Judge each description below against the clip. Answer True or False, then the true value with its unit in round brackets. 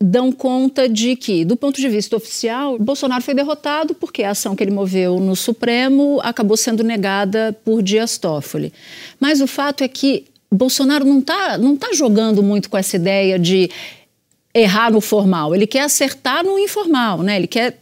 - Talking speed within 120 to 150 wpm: False (180 wpm)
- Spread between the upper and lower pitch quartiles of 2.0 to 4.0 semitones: False (5.1 semitones)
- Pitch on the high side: True (235 Hz)